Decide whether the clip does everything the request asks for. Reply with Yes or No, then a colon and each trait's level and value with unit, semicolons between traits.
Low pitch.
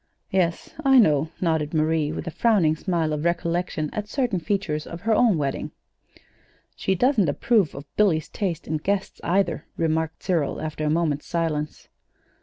No: medium, 170 Hz